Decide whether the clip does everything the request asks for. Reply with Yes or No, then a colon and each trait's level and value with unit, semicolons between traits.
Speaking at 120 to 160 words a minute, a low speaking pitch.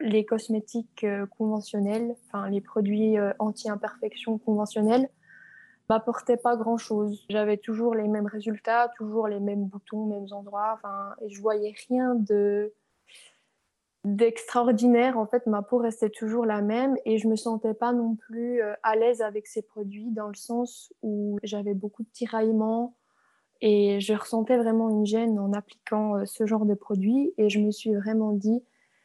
No: average, 155 wpm; high, 220 Hz